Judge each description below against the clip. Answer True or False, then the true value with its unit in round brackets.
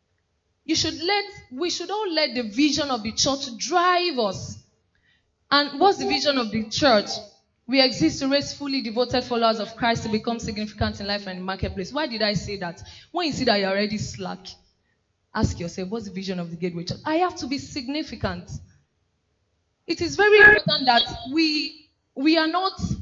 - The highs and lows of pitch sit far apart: True (7.5 semitones)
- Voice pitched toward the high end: True (255 Hz)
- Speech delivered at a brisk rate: False (195 wpm)